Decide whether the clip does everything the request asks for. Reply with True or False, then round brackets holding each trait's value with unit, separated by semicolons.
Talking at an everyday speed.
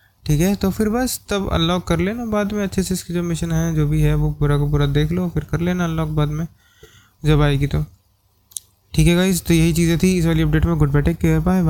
False (255 wpm)